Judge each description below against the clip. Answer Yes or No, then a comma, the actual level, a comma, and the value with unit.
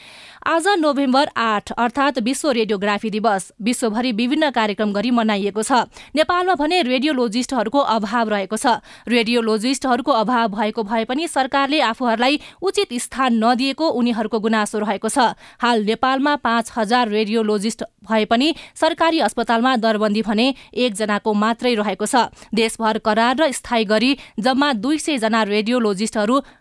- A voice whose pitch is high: Yes, high, 235 Hz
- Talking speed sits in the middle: No, slow, 130 wpm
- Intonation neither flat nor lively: Yes, average, 3.6 semitones